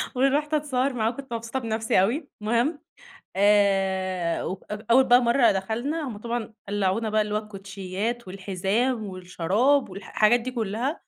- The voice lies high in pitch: Yes, high, 220 Hz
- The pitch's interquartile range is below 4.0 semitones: No, average, 4.3 semitones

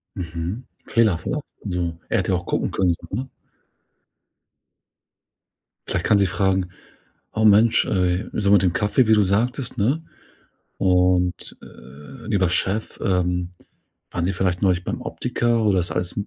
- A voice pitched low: Yes, very low, 95 Hz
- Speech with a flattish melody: No, average, 3.4 semitones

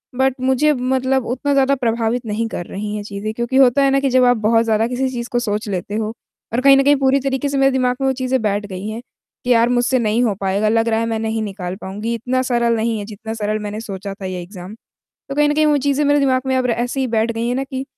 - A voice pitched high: Yes, high, 235 Hz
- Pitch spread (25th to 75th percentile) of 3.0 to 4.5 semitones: Yes, average, 3.5 semitones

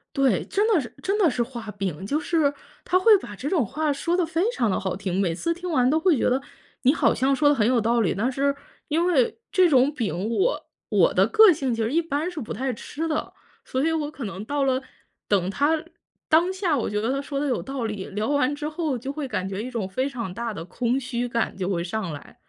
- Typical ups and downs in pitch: No, wide, 6.2 semitones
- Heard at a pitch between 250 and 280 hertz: Yes, very high, 265 Hz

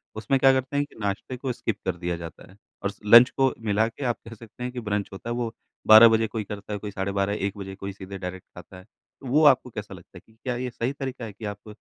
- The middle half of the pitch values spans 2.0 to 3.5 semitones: No, average, 3.9 semitones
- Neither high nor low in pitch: No, low, 110 Hz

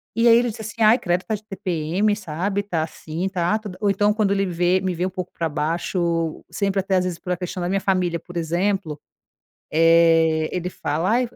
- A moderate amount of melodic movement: Yes, average, 3.2 semitones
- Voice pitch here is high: No, medium, 180 Hz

